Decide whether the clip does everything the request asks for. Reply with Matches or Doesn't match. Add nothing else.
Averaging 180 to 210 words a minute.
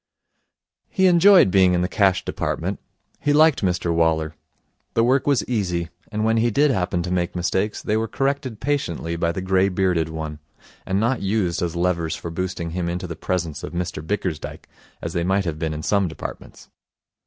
Matches